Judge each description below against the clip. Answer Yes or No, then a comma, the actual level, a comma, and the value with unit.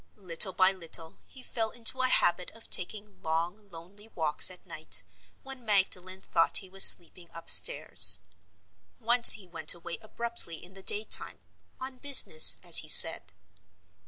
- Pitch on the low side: No, high, 190 Hz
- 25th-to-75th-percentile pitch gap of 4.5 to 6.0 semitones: Yes, average, 4.8 semitones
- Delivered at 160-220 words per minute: No, average, 150 wpm